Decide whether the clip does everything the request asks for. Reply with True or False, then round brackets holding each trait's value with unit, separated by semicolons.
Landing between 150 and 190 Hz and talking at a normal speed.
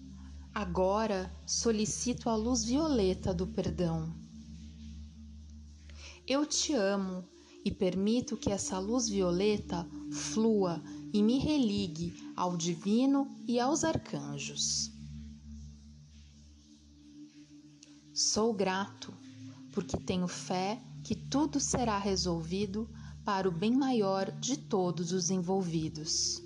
False (185 Hz; 95 wpm)